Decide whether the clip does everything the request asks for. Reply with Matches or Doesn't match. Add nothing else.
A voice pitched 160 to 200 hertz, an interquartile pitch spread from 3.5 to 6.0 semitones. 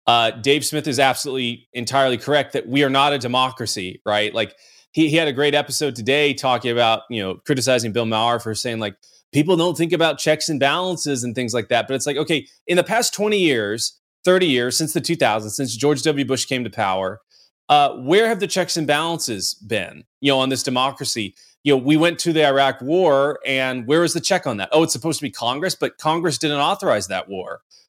Doesn't match